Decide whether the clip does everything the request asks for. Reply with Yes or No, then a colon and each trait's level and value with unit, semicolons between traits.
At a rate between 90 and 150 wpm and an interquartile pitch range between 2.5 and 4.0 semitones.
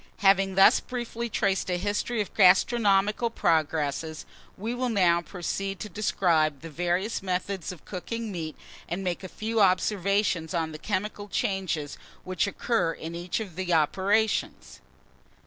Yes: average, 145 wpm; average, 3.5 semitones